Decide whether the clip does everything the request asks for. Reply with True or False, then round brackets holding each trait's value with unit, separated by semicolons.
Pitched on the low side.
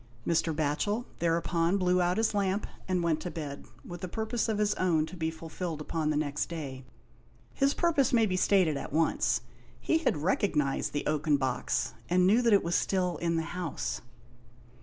False (170 Hz)